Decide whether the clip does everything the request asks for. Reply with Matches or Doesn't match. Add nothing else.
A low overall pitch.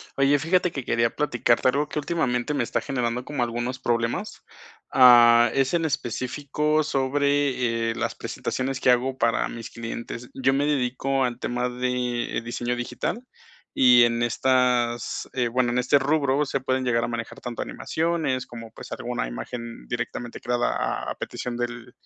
Matches